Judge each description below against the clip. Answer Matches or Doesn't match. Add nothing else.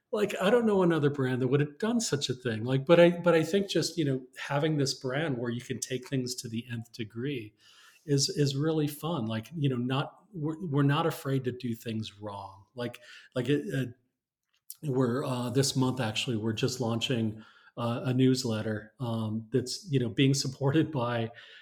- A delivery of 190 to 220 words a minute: Matches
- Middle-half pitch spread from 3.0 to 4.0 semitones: Matches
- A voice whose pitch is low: Matches